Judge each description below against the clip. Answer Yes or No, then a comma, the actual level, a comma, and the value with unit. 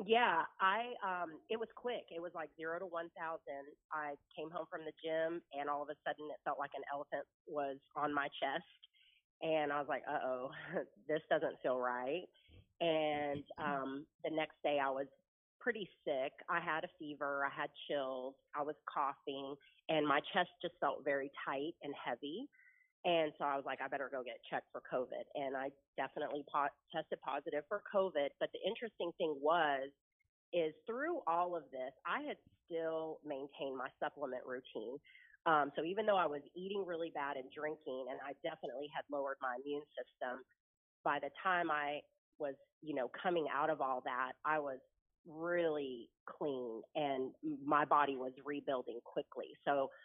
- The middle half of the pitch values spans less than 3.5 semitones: Yes, average, 3.1 semitones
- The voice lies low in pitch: No, medium, 150 Hz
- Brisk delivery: No, average, 175 wpm